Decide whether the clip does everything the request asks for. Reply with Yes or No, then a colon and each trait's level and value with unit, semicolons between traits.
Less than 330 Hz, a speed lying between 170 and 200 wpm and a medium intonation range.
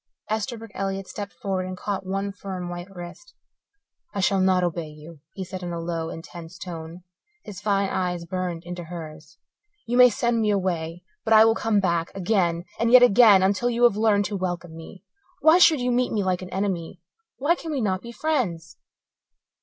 Yes: high, 190 Hz; average, 195 wpm; average, 3.9 semitones